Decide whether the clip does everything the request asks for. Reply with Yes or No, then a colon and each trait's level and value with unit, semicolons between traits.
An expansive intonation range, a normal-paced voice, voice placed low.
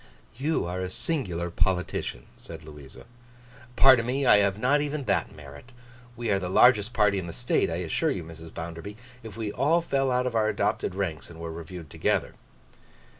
Yes: wide, 6.8 semitones; average, 185 wpm; low, 100 Hz